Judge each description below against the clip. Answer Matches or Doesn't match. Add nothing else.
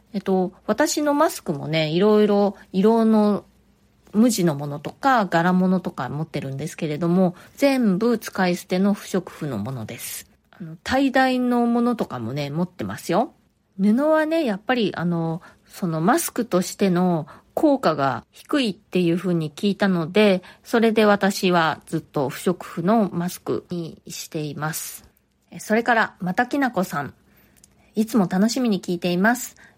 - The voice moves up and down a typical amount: Matches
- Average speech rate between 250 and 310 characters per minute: Matches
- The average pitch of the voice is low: Doesn't match